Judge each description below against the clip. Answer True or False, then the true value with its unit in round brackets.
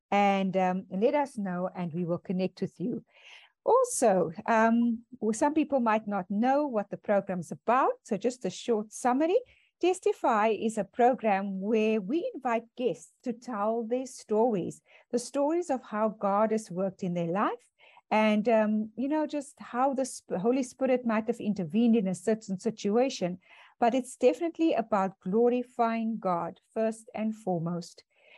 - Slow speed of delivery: False (165 wpm)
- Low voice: False (225 Hz)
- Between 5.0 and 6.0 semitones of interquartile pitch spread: False (4.1 semitones)